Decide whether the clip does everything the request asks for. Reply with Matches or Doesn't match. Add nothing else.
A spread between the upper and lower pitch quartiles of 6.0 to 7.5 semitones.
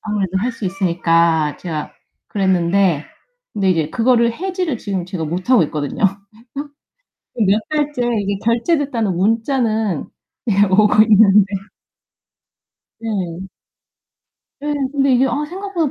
Doesn't match